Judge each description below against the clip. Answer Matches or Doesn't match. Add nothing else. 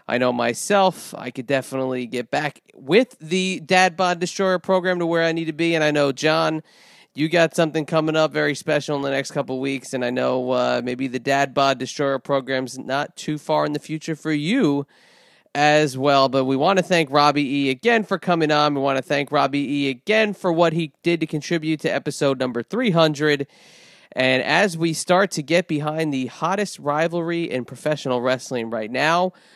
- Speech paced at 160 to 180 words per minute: Doesn't match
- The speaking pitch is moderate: Matches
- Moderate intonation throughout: Matches